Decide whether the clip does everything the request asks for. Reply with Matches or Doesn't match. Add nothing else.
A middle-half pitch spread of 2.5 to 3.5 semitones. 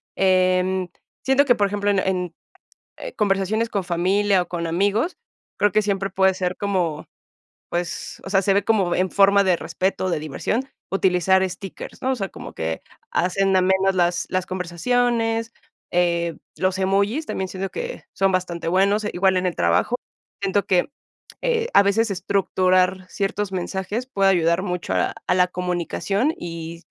Doesn't match